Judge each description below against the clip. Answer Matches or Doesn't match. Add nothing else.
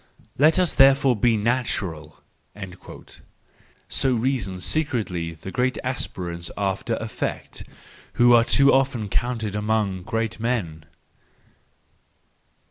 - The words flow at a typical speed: Doesn't match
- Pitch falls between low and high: Doesn't match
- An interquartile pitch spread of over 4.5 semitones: Matches